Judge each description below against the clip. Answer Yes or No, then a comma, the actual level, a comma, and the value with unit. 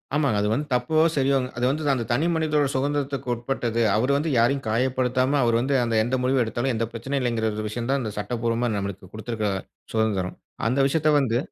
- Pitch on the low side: Yes, low, 125 Hz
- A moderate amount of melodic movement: Yes, average, 3.2 semitones